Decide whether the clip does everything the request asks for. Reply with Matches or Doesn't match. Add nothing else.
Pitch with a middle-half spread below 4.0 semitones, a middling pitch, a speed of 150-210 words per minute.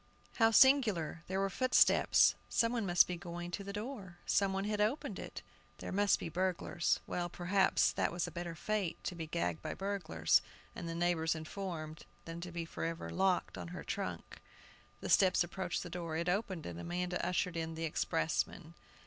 Matches